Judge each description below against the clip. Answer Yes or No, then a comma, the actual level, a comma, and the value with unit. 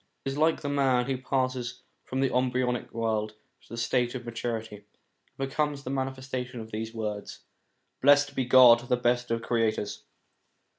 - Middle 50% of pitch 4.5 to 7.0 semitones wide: No, narrow, 2.4 semitones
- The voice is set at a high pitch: No, low, 125 Hz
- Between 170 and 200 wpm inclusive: Yes, average, 175 wpm